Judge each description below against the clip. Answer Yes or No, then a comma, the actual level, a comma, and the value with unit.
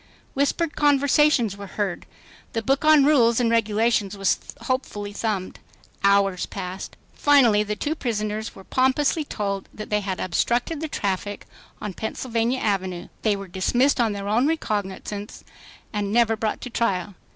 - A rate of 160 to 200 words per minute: No, average, 145 wpm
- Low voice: No, high, 215 Hz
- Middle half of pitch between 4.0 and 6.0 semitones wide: Yes, average, 4.3 semitones